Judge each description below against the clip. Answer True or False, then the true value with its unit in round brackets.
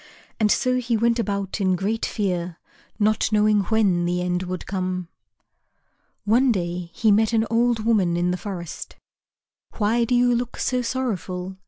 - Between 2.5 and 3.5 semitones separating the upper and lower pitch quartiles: False (4.1 semitones)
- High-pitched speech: True (210 Hz)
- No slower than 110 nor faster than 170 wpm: True (160 wpm)